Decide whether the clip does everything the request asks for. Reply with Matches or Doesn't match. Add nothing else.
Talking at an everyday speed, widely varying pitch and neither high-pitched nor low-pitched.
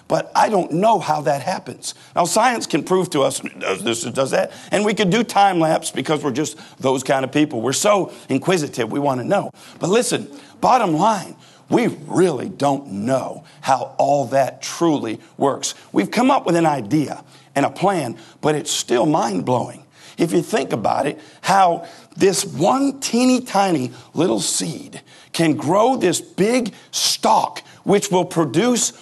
Matches